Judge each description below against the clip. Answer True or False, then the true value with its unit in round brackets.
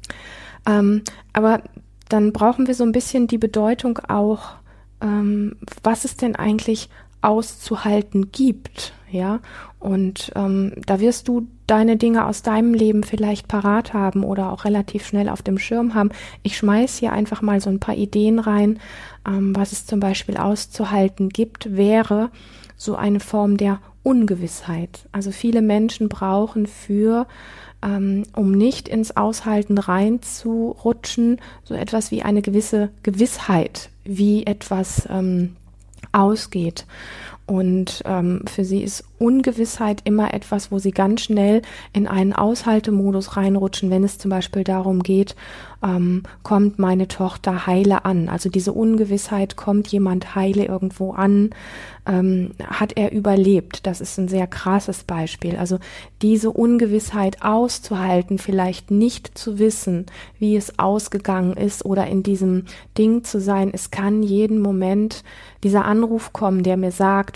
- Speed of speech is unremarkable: True (140 wpm)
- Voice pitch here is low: False (205 Hz)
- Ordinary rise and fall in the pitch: False (2.1 semitones)